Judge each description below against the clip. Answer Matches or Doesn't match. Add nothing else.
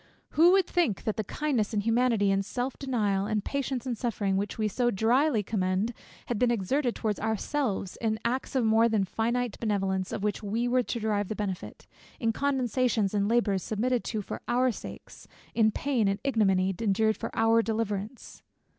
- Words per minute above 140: Matches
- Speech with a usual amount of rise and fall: Matches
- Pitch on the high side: Matches